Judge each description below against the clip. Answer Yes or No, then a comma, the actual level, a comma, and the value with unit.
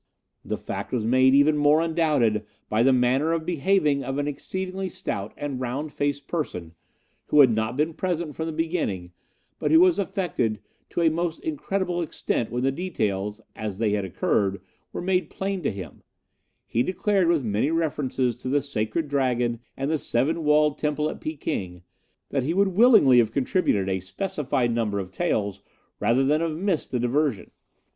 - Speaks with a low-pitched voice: No, medium, 145 Hz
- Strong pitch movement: Yes, wide, 6.0 semitones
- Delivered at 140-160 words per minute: No, average, 175 wpm